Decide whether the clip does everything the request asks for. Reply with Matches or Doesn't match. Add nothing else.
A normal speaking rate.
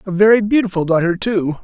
Matches